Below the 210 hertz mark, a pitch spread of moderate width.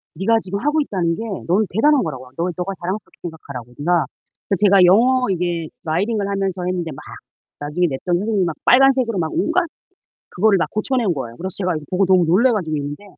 Yes: medium, 185 Hz; average, 4.4 semitones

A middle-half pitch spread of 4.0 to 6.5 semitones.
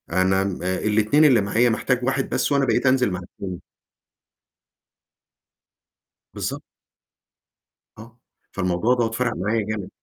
Yes: average, 4.6 semitones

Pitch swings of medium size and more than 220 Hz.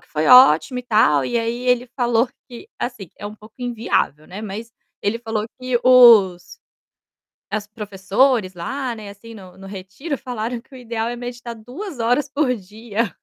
Yes: average, 3.4 semitones; high, 230 Hz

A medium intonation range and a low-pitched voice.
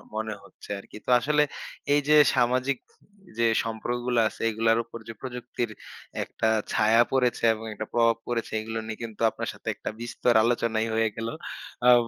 No: narrow, 1.5 semitones; low, 115 Hz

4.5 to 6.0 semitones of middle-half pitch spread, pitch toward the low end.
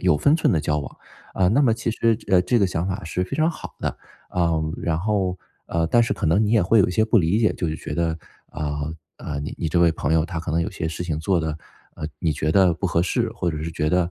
No: average, 4.0 semitones; very low, 85 Hz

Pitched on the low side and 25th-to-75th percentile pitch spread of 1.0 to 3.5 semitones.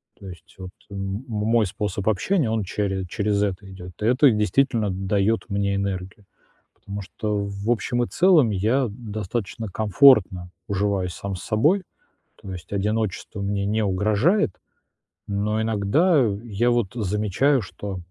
Yes: low, 105 Hz; narrow, 2.5 semitones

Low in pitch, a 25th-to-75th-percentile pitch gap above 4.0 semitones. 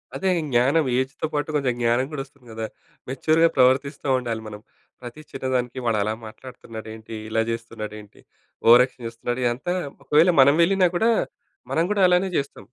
Yes: low, 130 Hz; average, 4.4 semitones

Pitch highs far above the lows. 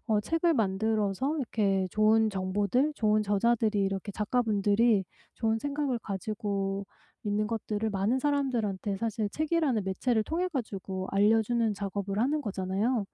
No: average, 3.2 semitones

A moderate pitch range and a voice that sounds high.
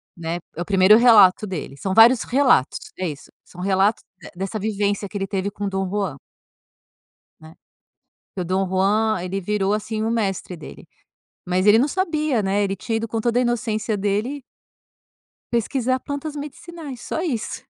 Yes: average, 3.7 semitones; high, 210 Hz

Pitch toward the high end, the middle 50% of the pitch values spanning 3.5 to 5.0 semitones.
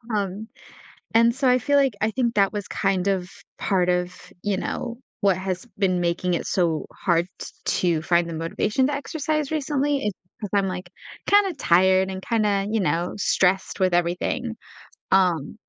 Yes: high, 195 Hz; average, 4.7 semitones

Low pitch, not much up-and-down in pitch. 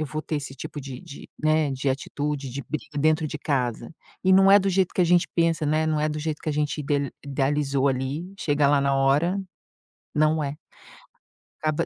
No: medium, 150 Hz; narrow, 2.2 semitones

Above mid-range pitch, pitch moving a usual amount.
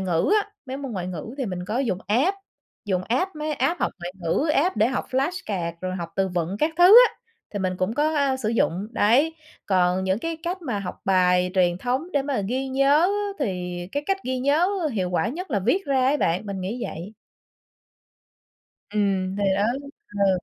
No: high, 215 Hz; wide, 7.2 semitones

